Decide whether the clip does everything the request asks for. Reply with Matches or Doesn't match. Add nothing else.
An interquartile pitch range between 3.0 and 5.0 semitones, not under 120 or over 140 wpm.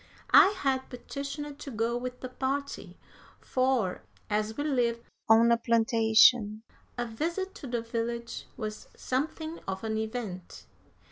Matches